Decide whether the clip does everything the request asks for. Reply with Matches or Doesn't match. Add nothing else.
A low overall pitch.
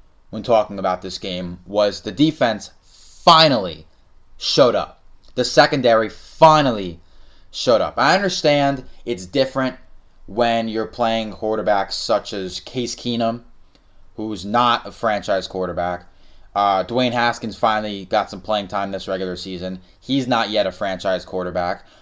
Matches